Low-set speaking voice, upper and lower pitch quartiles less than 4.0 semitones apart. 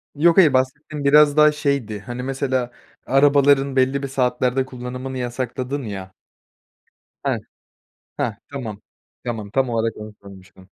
Yes: low, 130 Hz; average, 2.9 semitones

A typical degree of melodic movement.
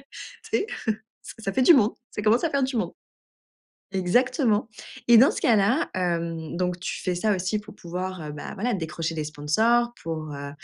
No: wide, 5.9 semitones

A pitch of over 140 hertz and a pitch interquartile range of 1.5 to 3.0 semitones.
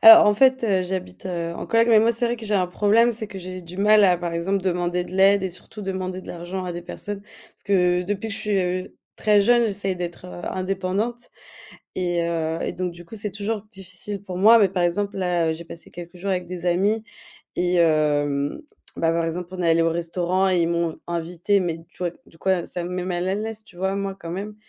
Yes: medium, 185 Hz; average, 2.7 semitones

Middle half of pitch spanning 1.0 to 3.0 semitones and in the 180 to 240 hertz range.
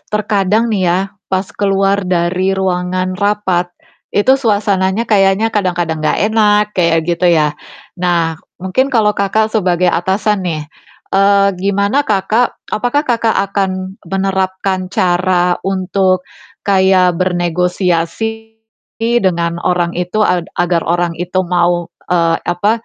Yes: narrow, 2.5 semitones; high, 190 Hz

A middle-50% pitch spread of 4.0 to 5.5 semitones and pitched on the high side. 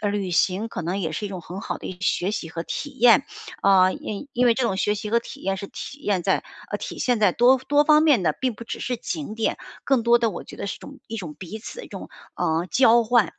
Yes: average, 4.6 semitones; high, 215 Hz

